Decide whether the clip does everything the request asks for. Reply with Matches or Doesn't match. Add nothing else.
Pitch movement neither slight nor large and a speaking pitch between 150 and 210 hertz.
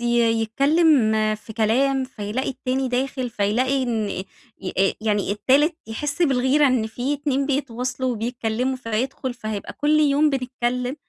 Doesn't match